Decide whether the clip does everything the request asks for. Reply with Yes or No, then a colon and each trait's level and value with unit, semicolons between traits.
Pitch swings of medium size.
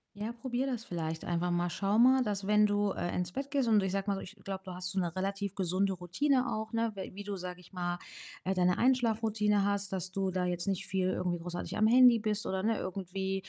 Yes: average, 3.0 semitones